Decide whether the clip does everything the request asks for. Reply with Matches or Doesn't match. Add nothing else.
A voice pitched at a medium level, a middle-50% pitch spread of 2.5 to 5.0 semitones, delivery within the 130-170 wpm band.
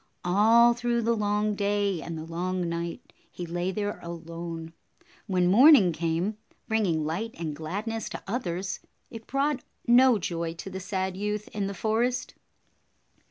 Doesn't match